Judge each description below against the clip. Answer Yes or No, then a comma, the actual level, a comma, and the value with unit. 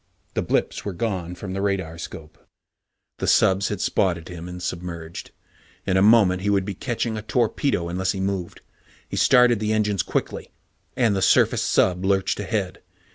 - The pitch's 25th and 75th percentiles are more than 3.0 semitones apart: No, average, 2.7 semitones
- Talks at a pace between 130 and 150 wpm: No, average, 175 wpm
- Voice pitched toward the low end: Yes, very low, 95 Hz